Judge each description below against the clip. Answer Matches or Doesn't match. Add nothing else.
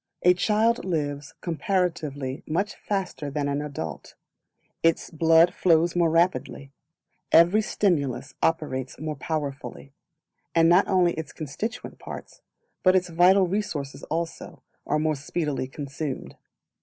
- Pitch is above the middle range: Doesn't match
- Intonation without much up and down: Doesn't match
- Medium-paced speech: Doesn't match